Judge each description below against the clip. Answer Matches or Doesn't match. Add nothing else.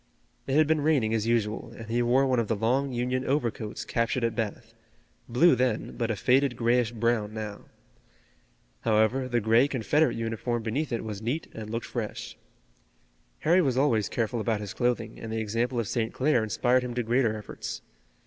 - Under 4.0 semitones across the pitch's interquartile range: Matches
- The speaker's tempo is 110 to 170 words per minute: Doesn't match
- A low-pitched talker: Matches